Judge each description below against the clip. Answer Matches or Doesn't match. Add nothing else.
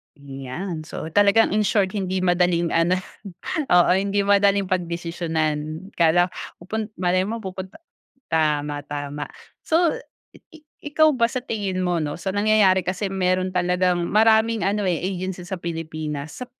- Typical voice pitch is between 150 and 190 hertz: Matches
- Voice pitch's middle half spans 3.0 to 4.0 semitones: Matches